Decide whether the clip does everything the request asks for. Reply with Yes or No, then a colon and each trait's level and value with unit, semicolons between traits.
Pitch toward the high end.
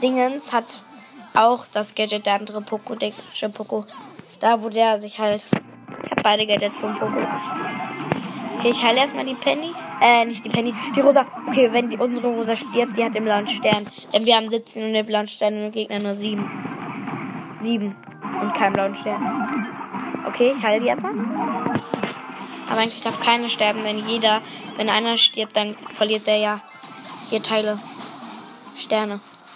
Yes: high, 220 Hz